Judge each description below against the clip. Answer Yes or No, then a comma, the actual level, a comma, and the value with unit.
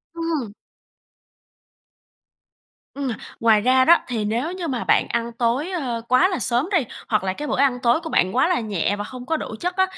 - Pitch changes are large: Yes, wide, 5.8 semitones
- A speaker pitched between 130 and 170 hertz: No, very high, 255 Hz